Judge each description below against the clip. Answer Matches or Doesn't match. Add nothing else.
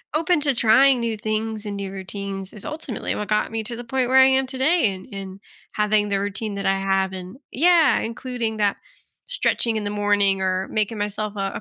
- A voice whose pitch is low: Doesn't match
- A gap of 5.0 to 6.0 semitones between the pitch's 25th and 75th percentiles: Doesn't match